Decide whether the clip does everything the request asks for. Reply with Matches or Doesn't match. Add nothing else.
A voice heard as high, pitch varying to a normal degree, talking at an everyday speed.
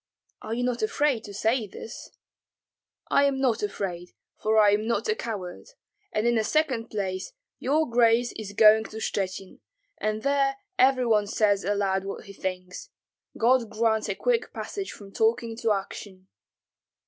Matches